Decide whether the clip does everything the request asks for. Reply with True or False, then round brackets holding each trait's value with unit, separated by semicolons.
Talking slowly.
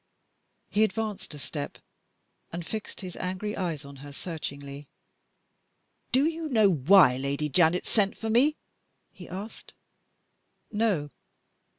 True (120 wpm)